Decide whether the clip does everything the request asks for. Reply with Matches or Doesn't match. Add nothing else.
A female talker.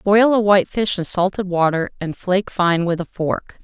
Matches